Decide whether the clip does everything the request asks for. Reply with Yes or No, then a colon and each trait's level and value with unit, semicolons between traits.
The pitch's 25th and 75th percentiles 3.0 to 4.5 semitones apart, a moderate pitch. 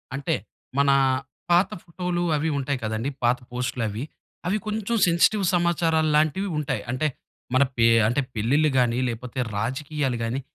No: wide, 5.6 semitones; medium, 145 Hz